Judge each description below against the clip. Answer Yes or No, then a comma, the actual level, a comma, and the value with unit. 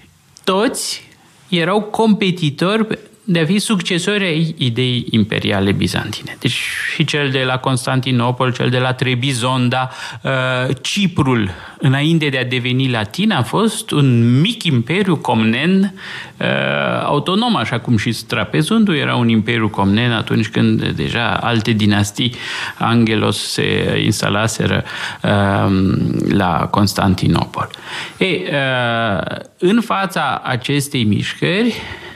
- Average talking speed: No, slow, 105 wpm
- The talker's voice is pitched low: Yes, low, 130 Hz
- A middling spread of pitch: No, wide, 6.8 semitones